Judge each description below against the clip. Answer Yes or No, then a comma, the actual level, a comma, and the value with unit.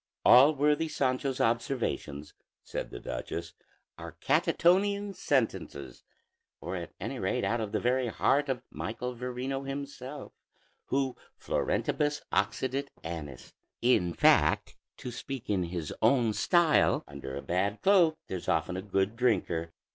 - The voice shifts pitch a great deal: Yes, wide, 7.1 semitones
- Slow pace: Yes, slow, 130 wpm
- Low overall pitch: Yes, low, 125 Hz